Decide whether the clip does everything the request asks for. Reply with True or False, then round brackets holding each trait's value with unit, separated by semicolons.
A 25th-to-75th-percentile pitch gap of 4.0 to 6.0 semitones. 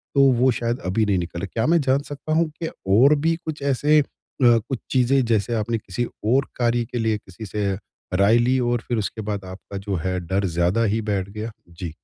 True (4.5 semitones)